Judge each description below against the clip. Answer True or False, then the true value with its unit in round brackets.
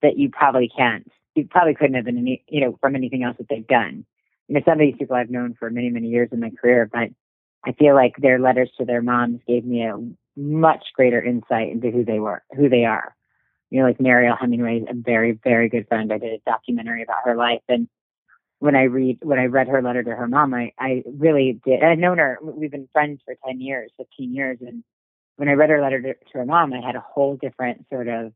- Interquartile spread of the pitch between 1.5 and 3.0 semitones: True (2.4 semitones)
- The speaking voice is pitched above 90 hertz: True (125 Hz)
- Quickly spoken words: True (245 wpm)